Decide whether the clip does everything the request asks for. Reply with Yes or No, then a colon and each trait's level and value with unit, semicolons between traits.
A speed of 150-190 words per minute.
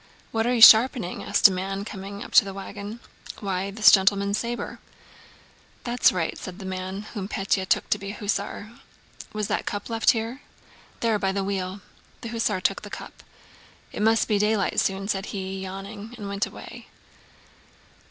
Yes: average, 175 wpm